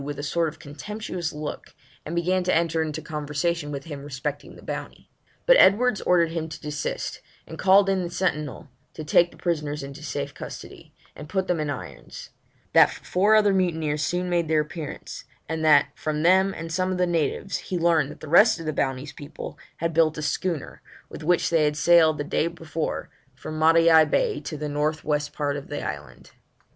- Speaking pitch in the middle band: Yes, medium, 160 Hz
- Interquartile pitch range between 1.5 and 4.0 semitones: Yes, average, 2.9 semitones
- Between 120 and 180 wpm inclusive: No, average, 200 wpm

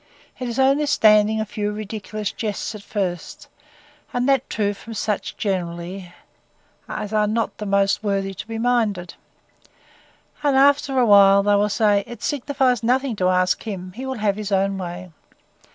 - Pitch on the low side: No, high, 210 Hz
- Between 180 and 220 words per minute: No, average, 170 wpm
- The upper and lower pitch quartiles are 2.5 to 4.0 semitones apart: Yes, average, 3.4 semitones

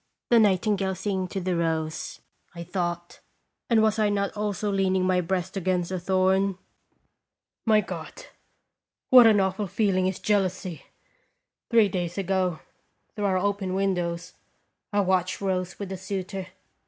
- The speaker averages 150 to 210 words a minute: No, average, 140 wpm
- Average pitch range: No, narrow, 1.9 semitones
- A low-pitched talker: No, high, 190 Hz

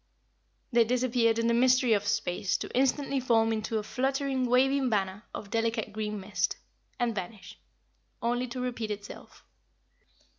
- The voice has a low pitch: No, high, 230 Hz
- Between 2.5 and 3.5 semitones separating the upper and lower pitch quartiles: Yes, average, 2.9 semitones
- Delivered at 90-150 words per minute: Yes, average, 145 wpm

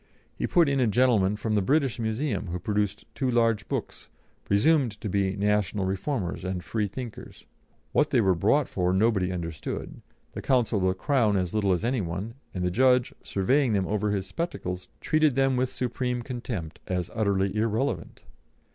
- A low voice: Yes, low, 105 Hz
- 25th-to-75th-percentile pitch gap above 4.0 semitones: Yes, average, 4.8 semitones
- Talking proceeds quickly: No, average, 175 wpm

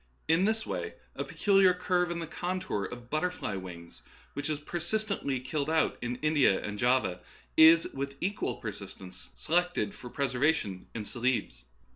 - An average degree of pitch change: No, wide, 6.8 semitones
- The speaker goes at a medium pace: Yes, average, 155 wpm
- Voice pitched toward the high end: No, medium, 145 Hz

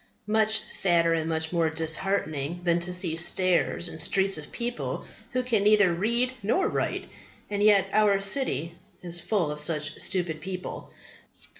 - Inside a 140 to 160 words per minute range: Yes, average, 155 wpm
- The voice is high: No, medium, 180 Hz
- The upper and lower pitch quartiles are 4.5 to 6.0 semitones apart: No, average, 4.1 semitones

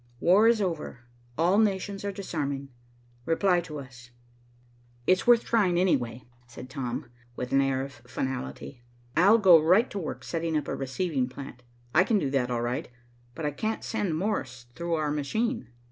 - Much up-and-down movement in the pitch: Yes, wide, 6.6 semitones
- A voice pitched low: No, medium, 155 Hz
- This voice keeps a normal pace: Yes, average, 170 wpm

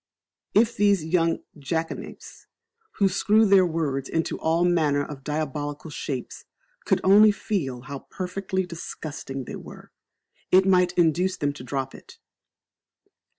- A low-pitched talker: No, medium, 165 Hz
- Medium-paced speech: No, slow, 130 wpm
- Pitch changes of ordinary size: Yes, average, 4.7 semitones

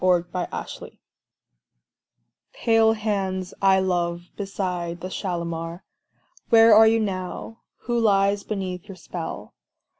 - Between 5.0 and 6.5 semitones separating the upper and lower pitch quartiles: No, average, 3.2 semitones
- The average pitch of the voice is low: No, high, 190 Hz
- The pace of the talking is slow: Yes, slow, 110 wpm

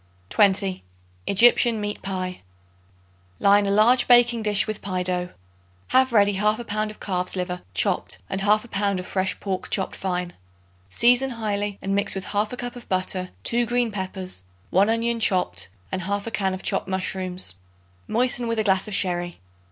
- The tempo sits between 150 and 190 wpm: Yes, average, 165 wpm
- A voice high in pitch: Yes, high, 200 Hz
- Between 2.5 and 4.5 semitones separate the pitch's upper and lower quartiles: Yes, average, 3.1 semitones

